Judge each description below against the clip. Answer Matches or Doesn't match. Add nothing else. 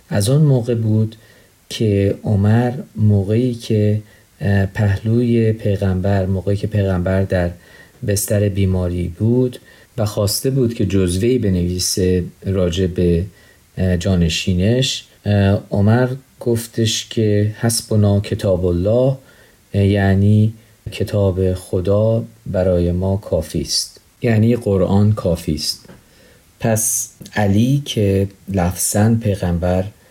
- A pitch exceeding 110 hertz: Doesn't match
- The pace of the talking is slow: Matches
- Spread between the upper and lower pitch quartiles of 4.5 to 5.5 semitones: Doesn't match